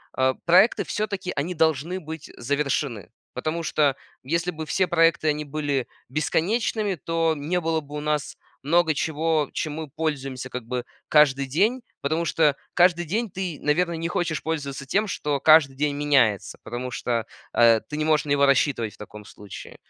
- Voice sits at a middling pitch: Yes, medium, 150 Hz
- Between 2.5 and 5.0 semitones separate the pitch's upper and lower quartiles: Yes, average, 3.3 semitones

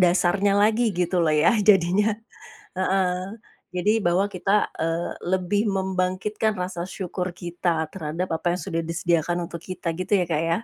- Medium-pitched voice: Yes, medium, 180 Hz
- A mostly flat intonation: Yes, narrow, 2.3 semitones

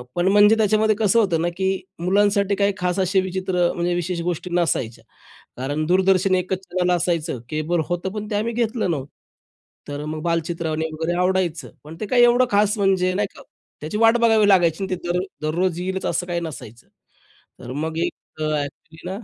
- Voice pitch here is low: No, medium, 180 Hz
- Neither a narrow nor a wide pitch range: Yes, average, 3.4 semitones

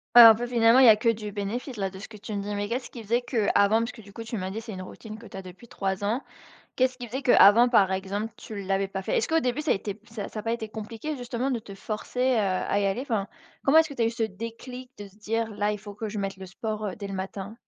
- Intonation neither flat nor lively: Yes, average, 3.0 semitones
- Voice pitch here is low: No, high, 220 Hz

